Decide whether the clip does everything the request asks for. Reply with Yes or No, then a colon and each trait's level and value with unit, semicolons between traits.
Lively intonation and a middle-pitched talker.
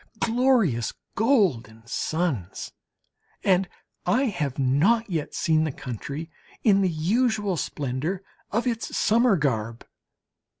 Yes: wide, 8.4 semitones; medium, 175 Hz